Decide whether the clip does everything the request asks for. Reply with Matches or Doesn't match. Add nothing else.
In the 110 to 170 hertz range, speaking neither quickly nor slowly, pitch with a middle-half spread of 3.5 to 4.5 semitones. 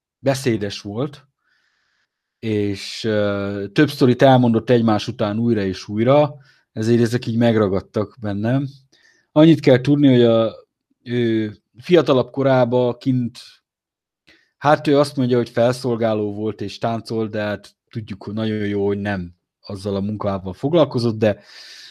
Matches